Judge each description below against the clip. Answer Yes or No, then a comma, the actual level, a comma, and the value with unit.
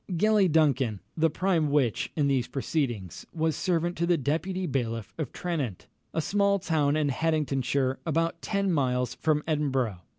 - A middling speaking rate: Yes, average, 155 wpm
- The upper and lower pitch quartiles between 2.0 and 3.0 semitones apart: No, average, 4.1 semitones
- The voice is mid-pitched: Yes, medium, 150 Hz